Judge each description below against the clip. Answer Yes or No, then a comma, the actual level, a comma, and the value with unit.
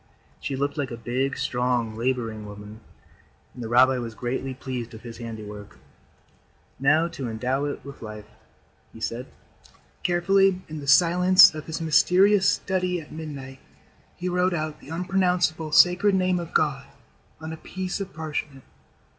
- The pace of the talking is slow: No, average, 155 wpm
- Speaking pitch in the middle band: Yes, medium, 145 Hz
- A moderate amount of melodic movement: No, wide, 6.3 semitones